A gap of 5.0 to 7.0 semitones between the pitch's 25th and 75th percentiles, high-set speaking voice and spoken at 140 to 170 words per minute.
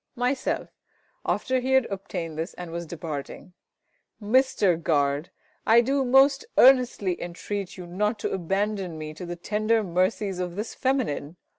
Yes: wide, 5.5 semitones; high, 195 Hz; average, 145 wpm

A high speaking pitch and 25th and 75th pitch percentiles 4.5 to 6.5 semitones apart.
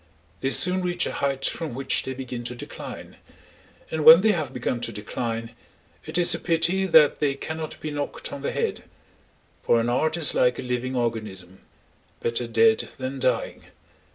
No: low, 130 Hz; average, 5.0 semitones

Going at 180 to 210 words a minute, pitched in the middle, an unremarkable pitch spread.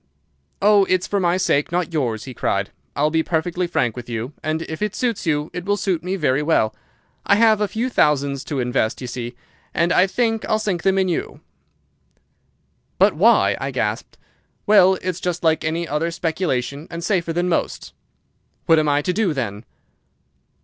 Yes: average, 190 wpm; medium, 165 Hz; average, 4.5 semitones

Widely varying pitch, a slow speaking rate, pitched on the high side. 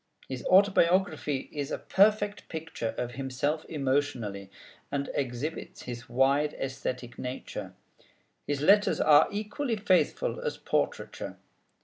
No: wide, 6.5 semitones; slow, 110 wpm; medium, 145 Hz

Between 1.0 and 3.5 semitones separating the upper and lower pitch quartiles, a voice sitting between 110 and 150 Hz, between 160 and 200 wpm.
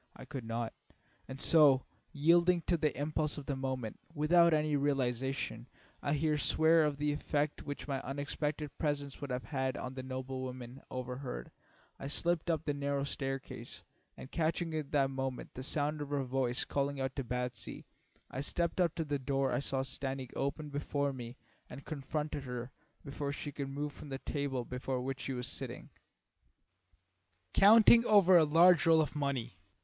Yes: narrow, 2.4 semitones; medium, 140 Hz; average, 175 wpm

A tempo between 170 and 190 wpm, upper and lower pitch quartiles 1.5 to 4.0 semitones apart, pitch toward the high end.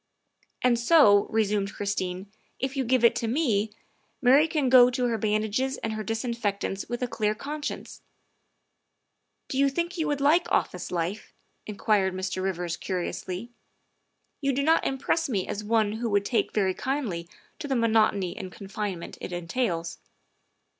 No: average, 175 wpm; average, 4.9 semitones; high, 220 Hz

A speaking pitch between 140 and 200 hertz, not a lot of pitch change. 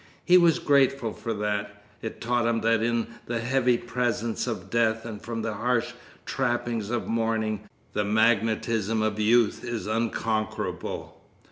No: low, 115 Hz; narrow, 1.7 semitones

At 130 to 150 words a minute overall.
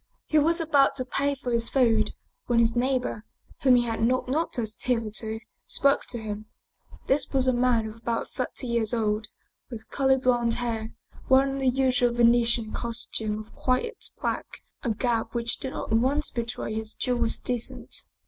No: average, 170 wpm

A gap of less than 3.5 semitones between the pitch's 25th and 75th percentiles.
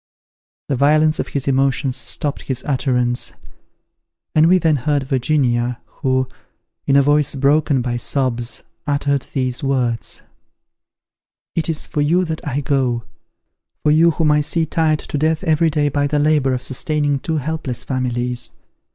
Yes: average, 3.1 semitones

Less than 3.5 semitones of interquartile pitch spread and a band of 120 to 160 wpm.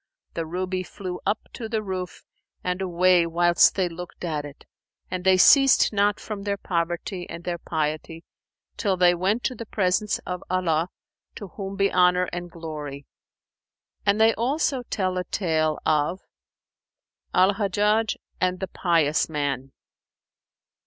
Yes: average, 2.9 semitones; average, 145 wpm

